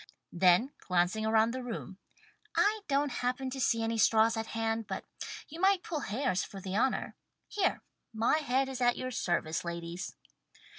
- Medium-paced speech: Yes, average, 165 wpm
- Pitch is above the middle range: Yes, high, 230 Hz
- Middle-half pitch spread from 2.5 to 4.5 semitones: No, average, 5.2 semitones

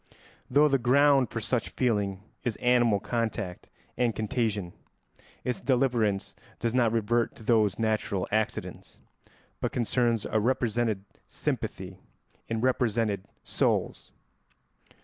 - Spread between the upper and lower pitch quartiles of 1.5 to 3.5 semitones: Yes, narrow, 2.6 semitones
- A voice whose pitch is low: Yes, low, 115 Hz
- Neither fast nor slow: No, slow, 110 wpm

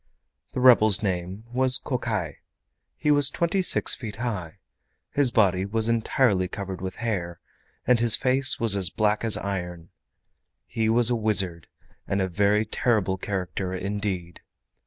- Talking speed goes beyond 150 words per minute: No, average, 145 wpm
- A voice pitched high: No, low, 105 Hz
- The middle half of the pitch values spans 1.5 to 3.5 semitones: No, average, 3.9 semitones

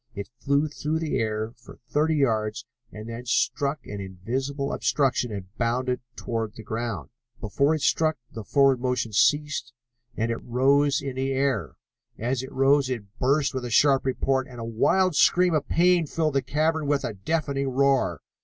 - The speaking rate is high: No, average, 175 wpm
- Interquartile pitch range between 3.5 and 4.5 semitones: Yes, average, 3.9 semitones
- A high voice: No, low, 130 Hz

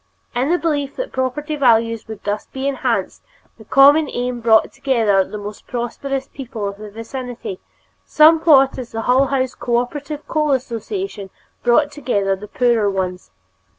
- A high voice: Yes, very high, 250 Hz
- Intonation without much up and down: No, average, 4.0 semitones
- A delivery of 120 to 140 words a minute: No, average, 150 wpm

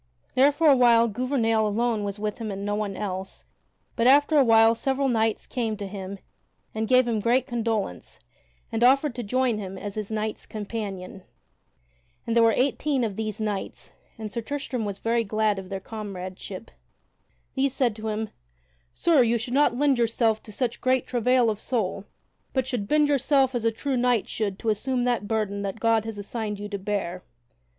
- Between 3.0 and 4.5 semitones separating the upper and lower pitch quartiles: Yes, average, 3.3 semitones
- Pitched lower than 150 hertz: No, high, 225 Hz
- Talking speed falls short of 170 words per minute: No, average, 190 wpm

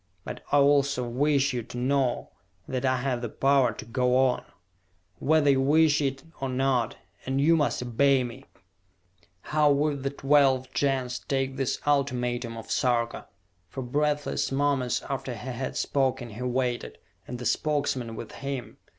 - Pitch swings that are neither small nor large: No, narrow, 2.2 semitones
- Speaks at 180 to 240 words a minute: No, average, 160 wpm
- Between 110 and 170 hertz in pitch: Yes, low, 135 Hz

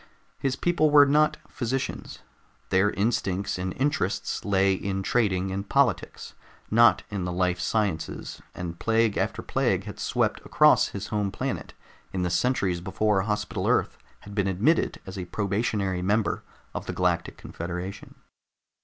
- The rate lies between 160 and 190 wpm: No, average, 145 wpm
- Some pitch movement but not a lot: Yes, average, 3.5 semitones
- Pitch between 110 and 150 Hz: No, low, 100 Hz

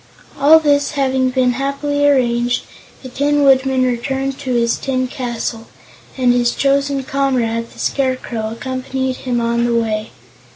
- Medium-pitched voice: No, very high, 260 Hz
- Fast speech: No, average, 140 wpm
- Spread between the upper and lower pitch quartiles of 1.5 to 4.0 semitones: Yes, narrow, 2.4 semitones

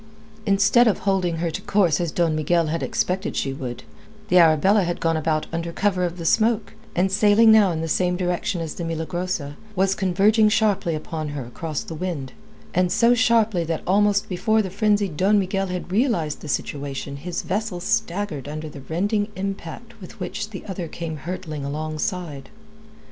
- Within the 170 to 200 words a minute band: Yes, average, 175 wpm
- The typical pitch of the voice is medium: Yes, medium, 180 Hz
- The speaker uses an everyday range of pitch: Yes, average, 4.2 semitones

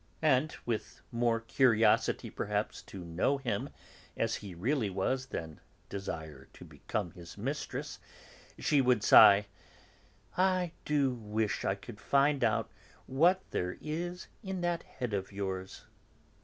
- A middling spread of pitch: No, wide, 6.4 semitones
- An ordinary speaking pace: No, slow, 130 wpm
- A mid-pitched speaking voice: No, low, 115 Hz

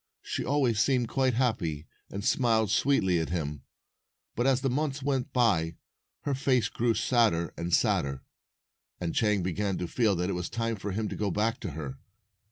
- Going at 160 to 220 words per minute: Yes, average, 180 wpm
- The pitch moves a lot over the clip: Yes, wide, 6.2 semitones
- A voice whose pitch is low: Yes, low, 110 Hz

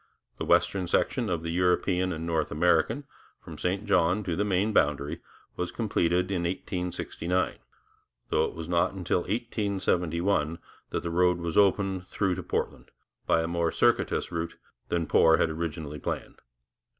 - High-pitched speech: No, very low, 90 Hz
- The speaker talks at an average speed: Yes, average, 155 wpm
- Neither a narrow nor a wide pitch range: No, narrow, 2.3 semitones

